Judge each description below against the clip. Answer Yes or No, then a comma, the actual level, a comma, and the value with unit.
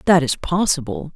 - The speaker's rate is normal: Yes, average, 155 wpm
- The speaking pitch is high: No, medium, 165 Hz